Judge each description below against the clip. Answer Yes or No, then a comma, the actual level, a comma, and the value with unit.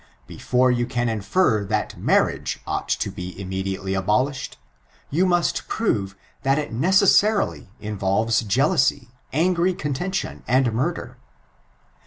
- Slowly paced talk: Yes, slow, 115 wpm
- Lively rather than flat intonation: Yes, wide, 8.4 semitones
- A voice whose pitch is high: No, low, 125 Hz